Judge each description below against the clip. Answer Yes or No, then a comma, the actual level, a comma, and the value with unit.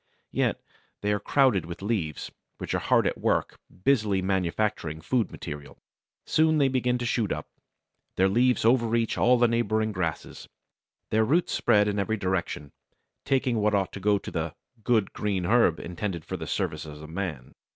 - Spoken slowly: No, average, 170 wpm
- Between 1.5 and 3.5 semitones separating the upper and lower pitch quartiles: No, average, 4.7 semitones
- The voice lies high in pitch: No, low, 105 Hz